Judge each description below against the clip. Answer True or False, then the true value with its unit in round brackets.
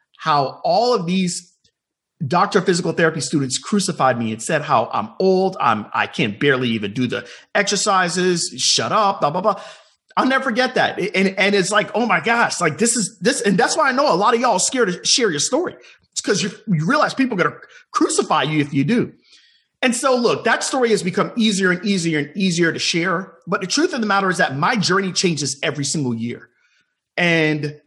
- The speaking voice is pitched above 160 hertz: True (185 Hz)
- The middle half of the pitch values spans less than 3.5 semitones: False (4.8 semitones)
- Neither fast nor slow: False (215 wpm)